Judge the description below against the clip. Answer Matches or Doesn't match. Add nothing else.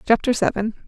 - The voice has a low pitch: Doesn't match